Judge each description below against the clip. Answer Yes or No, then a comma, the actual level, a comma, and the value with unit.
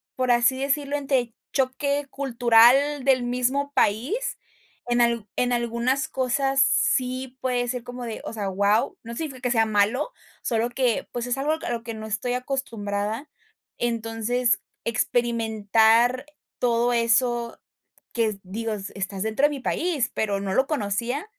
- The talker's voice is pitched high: Yes, high, 240 Hz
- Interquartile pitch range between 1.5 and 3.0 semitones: Yes, average, 2.7 semitones